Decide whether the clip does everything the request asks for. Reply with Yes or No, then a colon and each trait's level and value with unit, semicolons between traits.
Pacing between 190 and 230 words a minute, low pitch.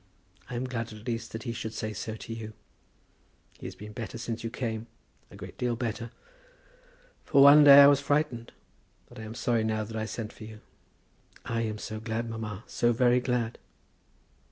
Yes: average, 195 wpm; low, 115 Hz